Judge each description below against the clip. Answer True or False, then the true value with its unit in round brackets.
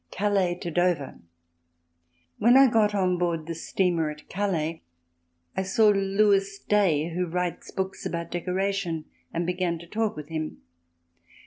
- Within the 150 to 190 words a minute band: False (140 wpm)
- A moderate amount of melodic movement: True (3.0 semitones)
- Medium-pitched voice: True (180 Hz)